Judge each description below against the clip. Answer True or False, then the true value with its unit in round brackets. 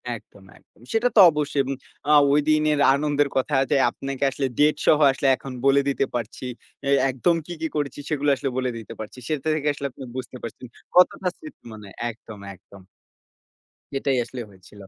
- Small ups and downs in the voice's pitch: False (3.1 semitones)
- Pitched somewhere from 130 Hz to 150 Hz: True (140 Hz)